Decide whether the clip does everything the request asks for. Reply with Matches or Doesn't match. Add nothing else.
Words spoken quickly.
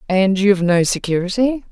Doesn't match